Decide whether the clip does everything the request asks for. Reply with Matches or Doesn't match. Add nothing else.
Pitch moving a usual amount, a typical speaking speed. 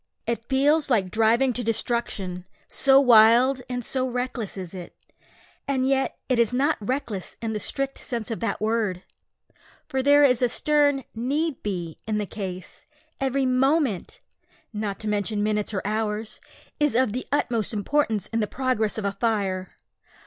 Matches